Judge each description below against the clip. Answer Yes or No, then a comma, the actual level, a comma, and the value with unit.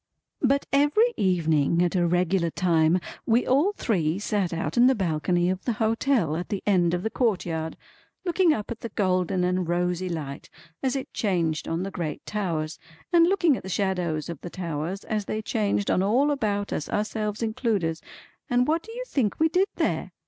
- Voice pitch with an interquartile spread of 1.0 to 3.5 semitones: No, wide, 5.6 semitones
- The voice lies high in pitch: Yes, high, 195 Hz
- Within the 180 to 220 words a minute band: Yes, average, 190 wpm